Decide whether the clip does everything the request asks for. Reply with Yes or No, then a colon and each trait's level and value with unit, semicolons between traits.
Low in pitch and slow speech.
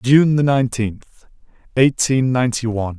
Yes: low, 125 Hz; slow, 100 wpm